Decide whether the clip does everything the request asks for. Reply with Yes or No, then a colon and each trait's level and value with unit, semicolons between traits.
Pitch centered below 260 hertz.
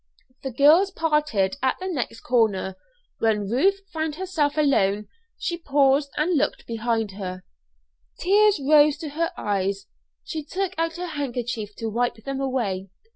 No: very high, 275 Hz